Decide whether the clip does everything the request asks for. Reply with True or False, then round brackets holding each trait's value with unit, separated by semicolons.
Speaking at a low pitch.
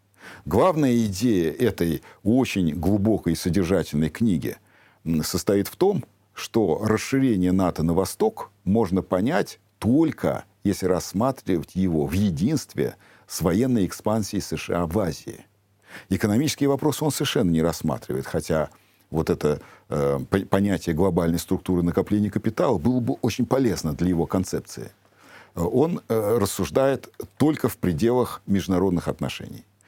True (95 Hz)